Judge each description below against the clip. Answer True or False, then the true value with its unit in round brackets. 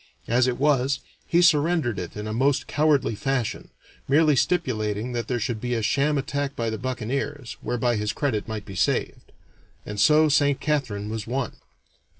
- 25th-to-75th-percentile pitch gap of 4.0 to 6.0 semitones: True (4.4 semitones)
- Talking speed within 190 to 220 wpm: False (170 wpm)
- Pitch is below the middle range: True (125 Hz)